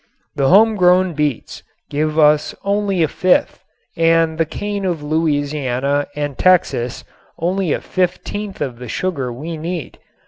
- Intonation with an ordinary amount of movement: Yes, average, 4.2 semitones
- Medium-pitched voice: Yes, medium, 160 Hz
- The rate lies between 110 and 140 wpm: Yes, slow, 135 wpm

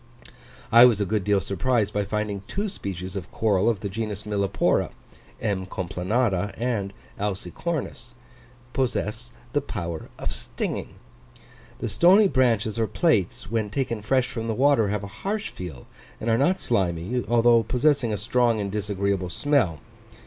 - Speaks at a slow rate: No, average, 155 wpm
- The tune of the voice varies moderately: Yes, average, 3.8 semitones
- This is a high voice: No, low, 110 Hz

